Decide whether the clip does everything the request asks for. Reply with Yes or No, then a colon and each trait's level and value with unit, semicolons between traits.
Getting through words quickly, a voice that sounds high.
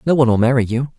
No: fast, 305 wpm; low, 125 Hz